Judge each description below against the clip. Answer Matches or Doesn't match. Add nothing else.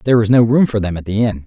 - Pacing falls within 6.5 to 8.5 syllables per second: Matches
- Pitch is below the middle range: Matches